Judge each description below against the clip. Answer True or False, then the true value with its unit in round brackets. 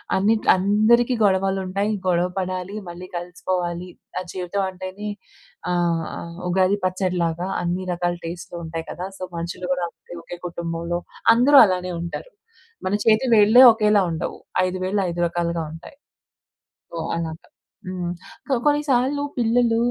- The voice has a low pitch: False (185 Hz)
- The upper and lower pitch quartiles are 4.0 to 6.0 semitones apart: False (3.0 semitones)